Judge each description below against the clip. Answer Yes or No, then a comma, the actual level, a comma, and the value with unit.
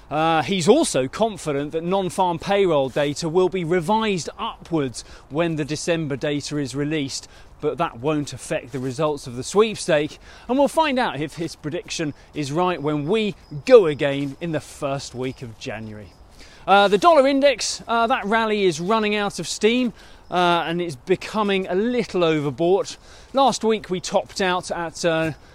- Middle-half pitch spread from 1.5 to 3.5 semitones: No, wide, 5.5 semitones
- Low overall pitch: No, medium, 170 Hz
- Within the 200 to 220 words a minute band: No, average, 170 wpm